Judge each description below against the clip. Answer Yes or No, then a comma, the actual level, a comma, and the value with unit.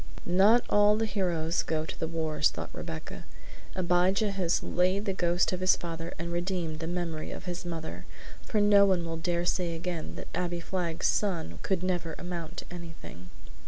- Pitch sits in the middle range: Yes, medium, 175 Hz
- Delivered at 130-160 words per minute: No, average, 180 wpm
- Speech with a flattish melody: Yes, narrow, 2.1 semitones